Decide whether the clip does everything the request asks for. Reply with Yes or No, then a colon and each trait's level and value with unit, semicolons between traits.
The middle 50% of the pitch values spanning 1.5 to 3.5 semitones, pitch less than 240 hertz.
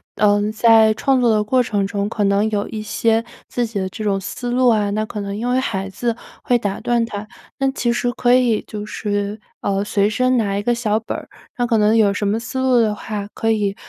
Yes: average, 2.8 semitones; high, 215 Hz